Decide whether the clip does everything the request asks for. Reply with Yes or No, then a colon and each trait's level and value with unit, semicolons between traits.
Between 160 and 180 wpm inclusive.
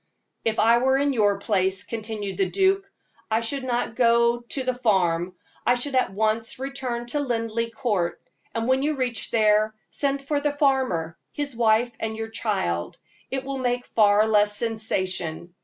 Yes: average, 170 wpm